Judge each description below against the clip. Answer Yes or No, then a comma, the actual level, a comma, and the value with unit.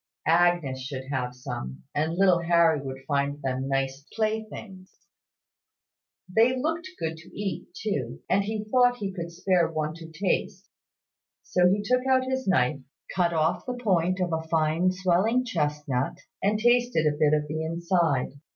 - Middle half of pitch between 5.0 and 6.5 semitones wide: Yes, wide, 5.5 semitones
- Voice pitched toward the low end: No, medium, 170 Hz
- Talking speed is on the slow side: No, average, 160 wpm